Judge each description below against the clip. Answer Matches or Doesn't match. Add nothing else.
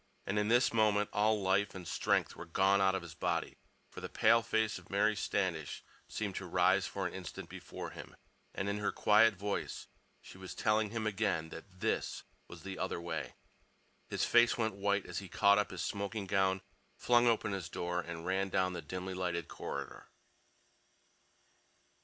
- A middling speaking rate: Matches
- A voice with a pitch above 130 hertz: Doesn't match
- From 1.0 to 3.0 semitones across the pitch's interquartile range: Matches